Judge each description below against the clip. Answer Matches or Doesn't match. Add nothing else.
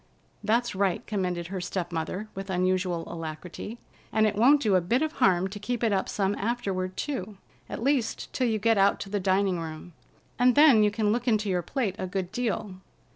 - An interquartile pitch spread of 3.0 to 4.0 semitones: Matches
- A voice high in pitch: Matches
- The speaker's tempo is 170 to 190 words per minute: Doesn't match